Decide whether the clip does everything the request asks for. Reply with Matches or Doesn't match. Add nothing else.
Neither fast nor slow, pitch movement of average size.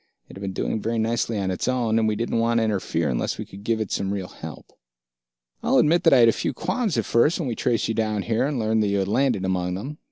Doesn't match